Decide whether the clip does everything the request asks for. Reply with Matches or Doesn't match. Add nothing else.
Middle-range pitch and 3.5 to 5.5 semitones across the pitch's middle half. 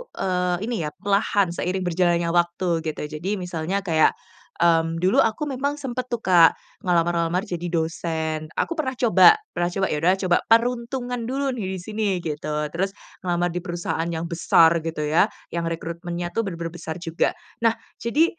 Matches